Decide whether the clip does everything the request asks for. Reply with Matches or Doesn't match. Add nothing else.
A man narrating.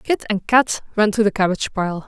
Doesn't match